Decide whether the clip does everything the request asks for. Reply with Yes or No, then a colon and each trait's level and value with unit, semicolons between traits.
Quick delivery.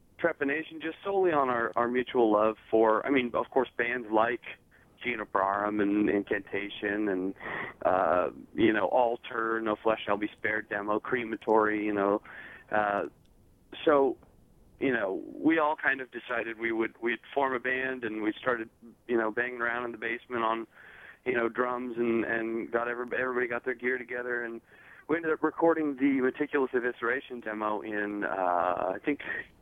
No: average, 170 wpm